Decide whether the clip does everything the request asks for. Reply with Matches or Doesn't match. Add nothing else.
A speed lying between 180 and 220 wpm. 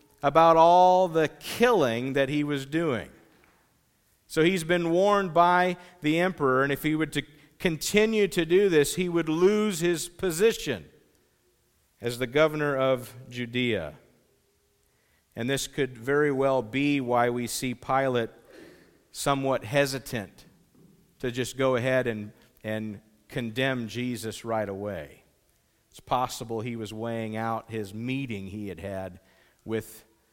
Doesn't match